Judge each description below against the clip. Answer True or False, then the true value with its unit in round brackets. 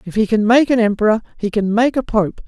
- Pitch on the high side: True (220 Hz)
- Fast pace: True (265 wpm)